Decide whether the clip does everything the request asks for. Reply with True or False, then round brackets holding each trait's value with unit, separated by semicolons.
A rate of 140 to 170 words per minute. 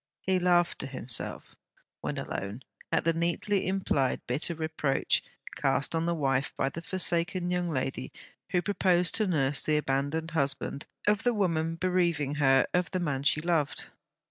True (160 wpm)